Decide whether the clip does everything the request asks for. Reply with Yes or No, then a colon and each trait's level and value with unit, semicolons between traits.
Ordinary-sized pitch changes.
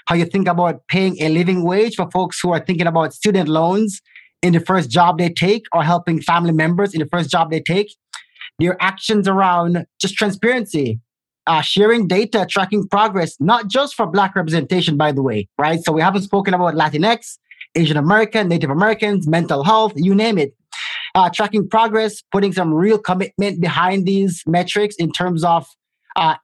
Yes: average, 3.4 semitones